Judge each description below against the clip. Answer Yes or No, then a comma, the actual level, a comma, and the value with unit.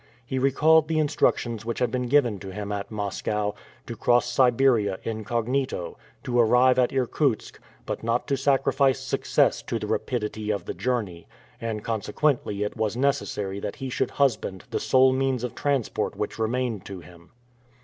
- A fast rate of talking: No, average, 165 wpm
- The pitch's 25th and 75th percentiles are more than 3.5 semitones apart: Yes, average, 3.9 semitones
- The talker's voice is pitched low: Yes, low, 120 Hz